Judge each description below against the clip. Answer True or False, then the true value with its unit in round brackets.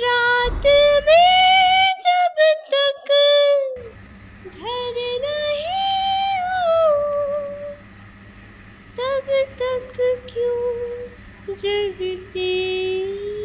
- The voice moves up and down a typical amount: False (7.7 semitones)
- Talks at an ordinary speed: False (50 wpm)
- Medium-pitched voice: False (375 Hz)